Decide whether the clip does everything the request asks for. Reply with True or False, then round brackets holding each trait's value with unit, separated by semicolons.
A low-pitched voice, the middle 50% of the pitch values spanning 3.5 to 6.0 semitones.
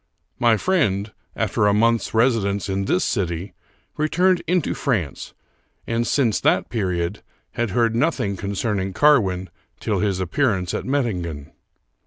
True (105 Hz; 4.4 semitones)